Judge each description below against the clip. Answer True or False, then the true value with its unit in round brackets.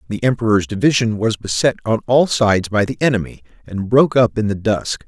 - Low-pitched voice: True (110 Hz)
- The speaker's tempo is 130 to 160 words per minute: False (200 wpm)